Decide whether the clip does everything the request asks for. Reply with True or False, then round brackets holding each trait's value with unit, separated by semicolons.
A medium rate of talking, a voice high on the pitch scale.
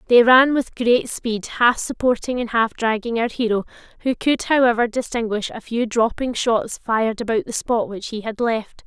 True (190 wpm; 230 Hz)